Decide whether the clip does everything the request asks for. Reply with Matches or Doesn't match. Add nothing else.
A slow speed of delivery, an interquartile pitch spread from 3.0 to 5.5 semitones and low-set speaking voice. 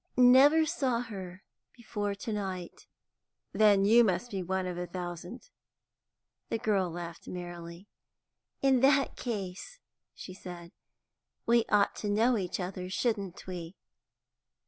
Doesn't match